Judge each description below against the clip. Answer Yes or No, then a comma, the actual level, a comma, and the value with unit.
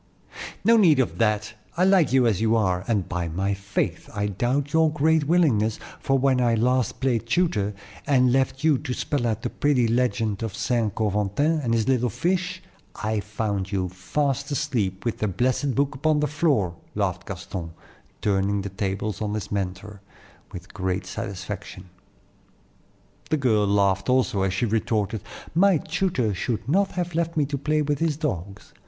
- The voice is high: No, low, 115 Hz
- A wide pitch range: Yes, wide, 6.2 semitones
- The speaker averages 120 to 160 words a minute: No, average, 170 wpm